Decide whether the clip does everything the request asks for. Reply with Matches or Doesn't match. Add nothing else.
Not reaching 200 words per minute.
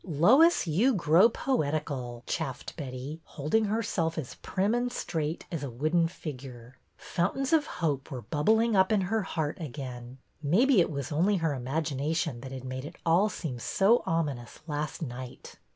Matches